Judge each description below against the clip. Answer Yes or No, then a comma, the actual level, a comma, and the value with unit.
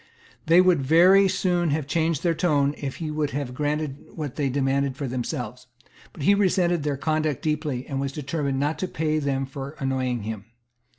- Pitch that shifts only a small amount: No, average, 3.1 semitones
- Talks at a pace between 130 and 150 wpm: No, average, 185 wpm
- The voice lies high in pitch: No, medium, 145 Hz